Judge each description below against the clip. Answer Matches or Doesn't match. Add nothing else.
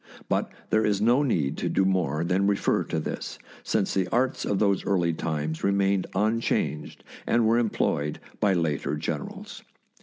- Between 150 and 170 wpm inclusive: Matches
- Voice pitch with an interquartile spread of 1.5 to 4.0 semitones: Doesn't match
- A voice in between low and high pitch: Doesn't match